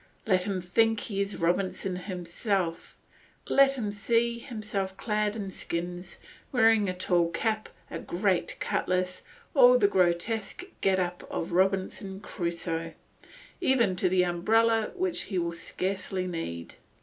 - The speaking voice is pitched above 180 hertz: Yes, high, 190 Hz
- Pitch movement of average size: Yes, average, 3.6 semitones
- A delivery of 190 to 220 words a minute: No, slow, 135 wpm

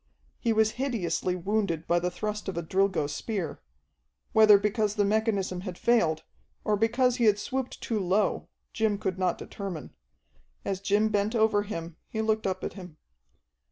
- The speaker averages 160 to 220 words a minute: Yes, average, 165 wpm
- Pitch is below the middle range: No, high, 205 Hz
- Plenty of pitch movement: No, average, 3.0 semitones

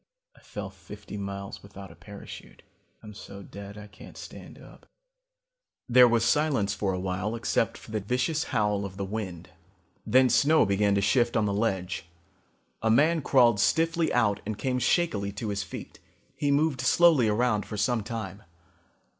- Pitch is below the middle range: Yes, low, 105 Hz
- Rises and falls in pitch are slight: No, average, 4.0 semitones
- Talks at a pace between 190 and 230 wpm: No, average, 170 wpm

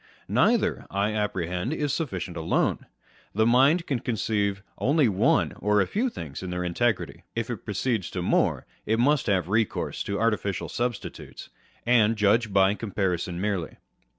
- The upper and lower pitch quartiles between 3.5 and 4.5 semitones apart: Yes, average, 4.0 semitones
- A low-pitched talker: Yes, low, 105 Hz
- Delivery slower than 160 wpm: Yes, average, 150 wpm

